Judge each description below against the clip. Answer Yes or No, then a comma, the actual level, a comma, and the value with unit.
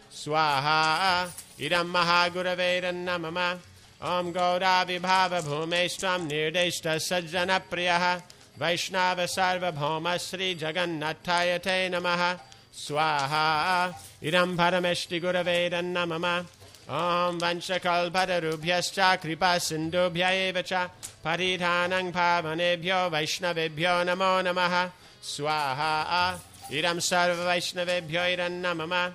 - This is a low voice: No, medium, 175 Hz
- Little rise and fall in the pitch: Yes, narrow, 1.5 semitones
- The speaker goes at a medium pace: No, slow, 60 wpm